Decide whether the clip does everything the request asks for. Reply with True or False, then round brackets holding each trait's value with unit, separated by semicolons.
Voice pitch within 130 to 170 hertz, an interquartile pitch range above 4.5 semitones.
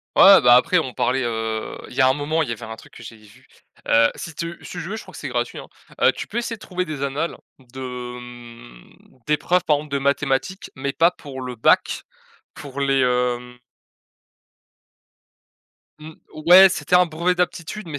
True (140 Hz; 5.4 semitones)